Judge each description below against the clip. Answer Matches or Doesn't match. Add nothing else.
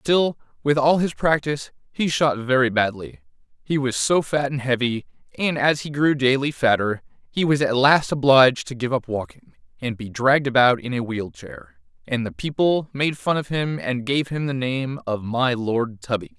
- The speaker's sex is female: Doesn't match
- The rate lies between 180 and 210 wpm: Matches